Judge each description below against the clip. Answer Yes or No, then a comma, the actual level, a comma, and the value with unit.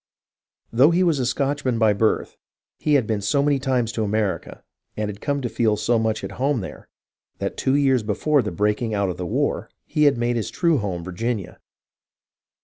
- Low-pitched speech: Yes, low, 115 Hz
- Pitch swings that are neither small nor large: Yes, average, 4.8 semitones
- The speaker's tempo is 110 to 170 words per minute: No, fast, 205 wpm